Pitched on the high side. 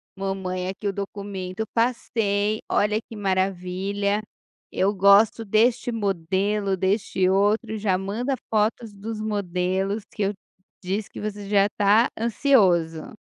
Yes: high, 200 Hz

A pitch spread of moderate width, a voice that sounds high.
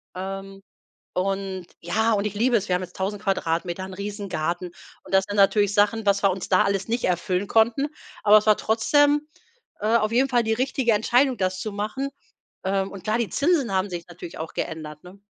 Yes: average, 3.0 semitones; high, 200 Hz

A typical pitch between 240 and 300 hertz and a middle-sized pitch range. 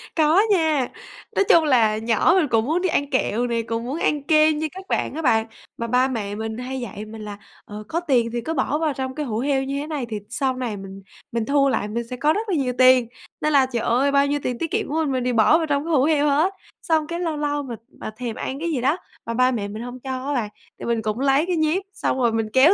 Yes: very high, 265 Hz; average, 4.6 semitones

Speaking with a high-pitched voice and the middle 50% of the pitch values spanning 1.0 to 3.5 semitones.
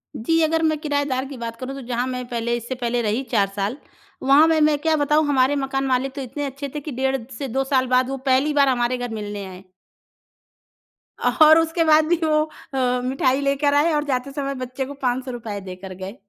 Yes: very high, 265 Hz; average, 2.9 semitones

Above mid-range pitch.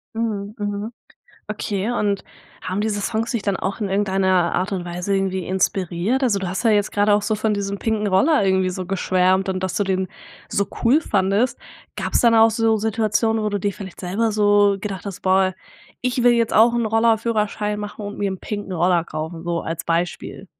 Yes: high, 205 Hz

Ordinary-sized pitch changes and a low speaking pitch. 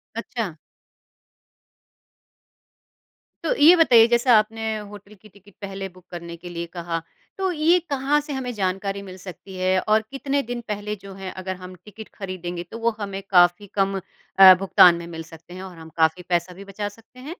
No: average, 3.9 semitones; high, 195 Hz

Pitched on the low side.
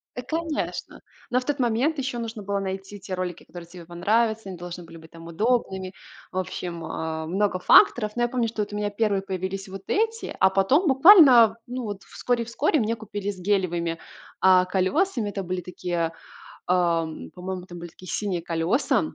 No: high, 195 Hz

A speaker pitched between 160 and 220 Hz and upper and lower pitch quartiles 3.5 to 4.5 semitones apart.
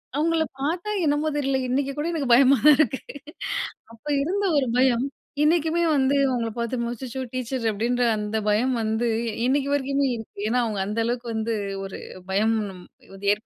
No: very high, 255 Hz; average, 3.9 semitones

